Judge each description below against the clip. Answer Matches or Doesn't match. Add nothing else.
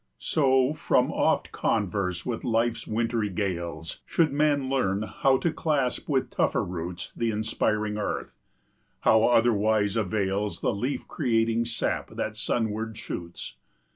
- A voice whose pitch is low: Matches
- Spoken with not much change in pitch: Doesn't match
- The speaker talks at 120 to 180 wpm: Matches